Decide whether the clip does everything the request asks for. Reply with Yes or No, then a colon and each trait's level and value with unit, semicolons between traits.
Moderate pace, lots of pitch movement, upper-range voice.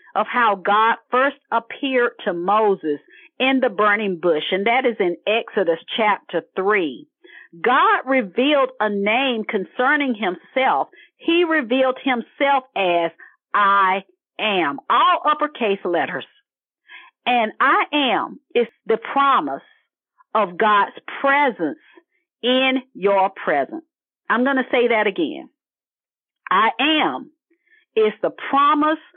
No: slow, 115 wpm; wide, 6.4 semitones; very high, 260 Hz